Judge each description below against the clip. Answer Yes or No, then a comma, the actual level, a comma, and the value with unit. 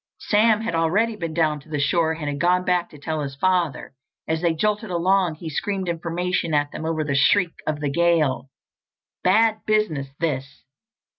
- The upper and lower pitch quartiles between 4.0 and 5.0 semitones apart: No, average, 3.4 semitones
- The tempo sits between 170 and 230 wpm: Yes, average, 180 wpm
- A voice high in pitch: No, medium, 165 Hz